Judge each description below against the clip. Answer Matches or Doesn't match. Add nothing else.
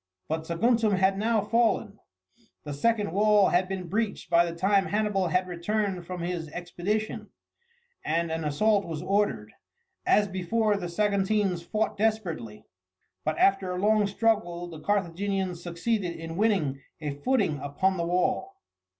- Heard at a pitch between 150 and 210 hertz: Matches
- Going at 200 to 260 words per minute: Doesn't match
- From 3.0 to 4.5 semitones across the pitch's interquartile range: Matches